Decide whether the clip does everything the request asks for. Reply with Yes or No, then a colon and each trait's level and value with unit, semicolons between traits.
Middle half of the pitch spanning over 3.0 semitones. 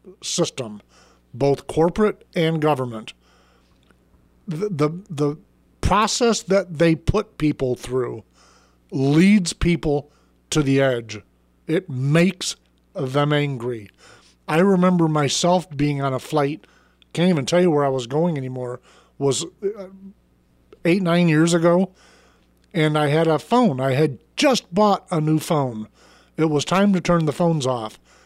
Yes: average, 5.3 semitones